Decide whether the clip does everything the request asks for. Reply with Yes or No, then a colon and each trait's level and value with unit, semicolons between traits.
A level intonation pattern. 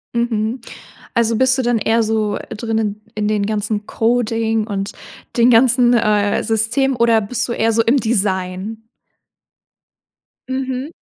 Yes: narrow, 2.1 semitones